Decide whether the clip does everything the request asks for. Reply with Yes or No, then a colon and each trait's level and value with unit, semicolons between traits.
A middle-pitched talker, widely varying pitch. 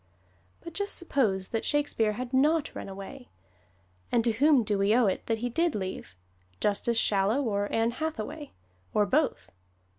No: high, 230 Hz; wide, 5.8 semitones